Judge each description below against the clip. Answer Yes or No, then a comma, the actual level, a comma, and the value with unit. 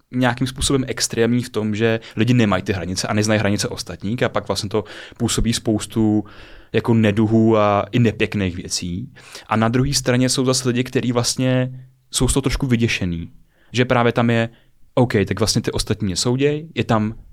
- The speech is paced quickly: Yes, fast, 180 wpm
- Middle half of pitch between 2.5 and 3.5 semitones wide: Yes, average, 2.8 semitones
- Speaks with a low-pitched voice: Yes, low, 115 Hz